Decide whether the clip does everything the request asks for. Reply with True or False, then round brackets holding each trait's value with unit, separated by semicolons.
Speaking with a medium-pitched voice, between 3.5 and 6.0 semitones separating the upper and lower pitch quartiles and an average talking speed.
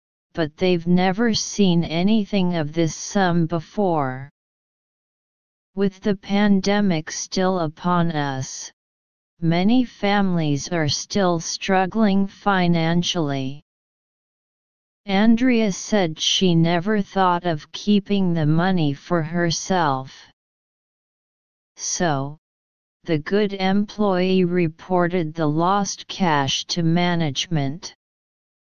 False (175 Hz; 3.8 semitones; 90 wpm)